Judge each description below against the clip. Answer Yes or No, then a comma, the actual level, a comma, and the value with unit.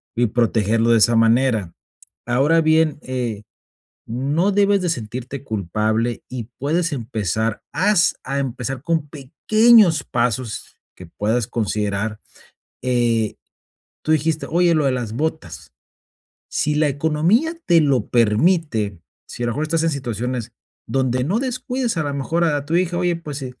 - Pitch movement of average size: No, wide, 6.0 semitones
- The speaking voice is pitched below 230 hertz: Yes, low, 135 Hz